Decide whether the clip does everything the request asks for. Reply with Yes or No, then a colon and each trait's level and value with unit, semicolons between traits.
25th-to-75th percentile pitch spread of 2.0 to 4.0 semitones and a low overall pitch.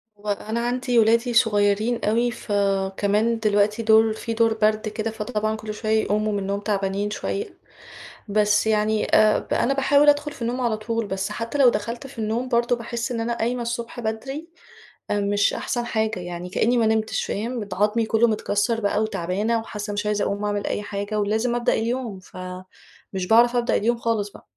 No: narrow, 2.4 semitones; high, 220 Hz